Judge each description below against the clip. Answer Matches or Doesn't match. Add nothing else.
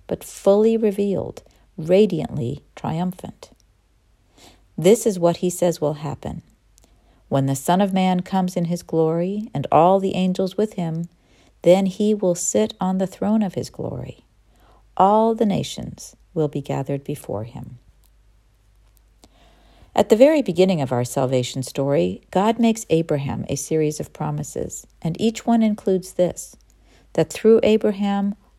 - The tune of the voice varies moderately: Doesn't match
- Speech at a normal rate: Matches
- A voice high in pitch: Doesn't match